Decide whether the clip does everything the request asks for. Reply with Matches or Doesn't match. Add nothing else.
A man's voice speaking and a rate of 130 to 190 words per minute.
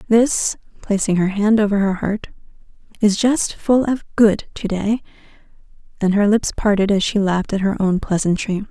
Doesn't match